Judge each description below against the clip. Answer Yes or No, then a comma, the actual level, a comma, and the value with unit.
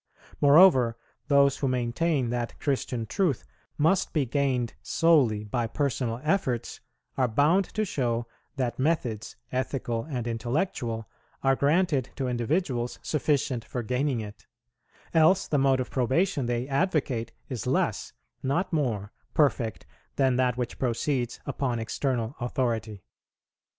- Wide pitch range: No, average, 3.5 semitones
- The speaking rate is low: Yes, slow, 125 wpm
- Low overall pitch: Yes, low, 130 Hz